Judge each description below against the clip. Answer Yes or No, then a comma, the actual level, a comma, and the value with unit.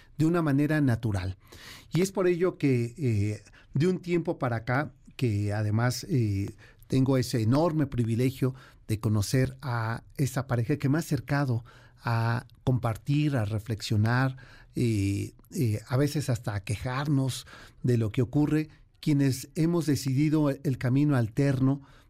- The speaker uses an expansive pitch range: No, average, 4.0 semitones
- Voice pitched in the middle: No, low, 130 Hz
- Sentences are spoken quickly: No, average, 140 wpm